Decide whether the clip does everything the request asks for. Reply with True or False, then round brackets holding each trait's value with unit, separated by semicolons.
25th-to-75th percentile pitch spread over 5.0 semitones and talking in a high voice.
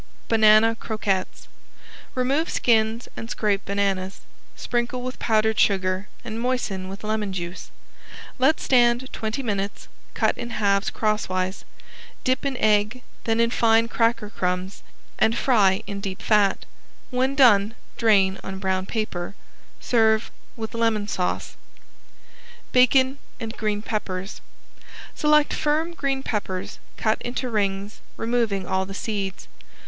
False (3.3 semitones; 220 Hz)